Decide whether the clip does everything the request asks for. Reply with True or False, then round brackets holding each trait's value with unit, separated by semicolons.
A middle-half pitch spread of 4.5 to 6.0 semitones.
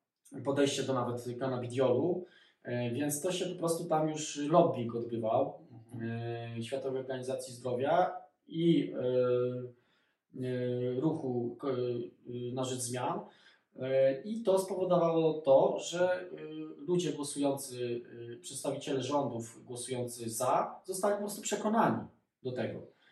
True (4.9 semitones)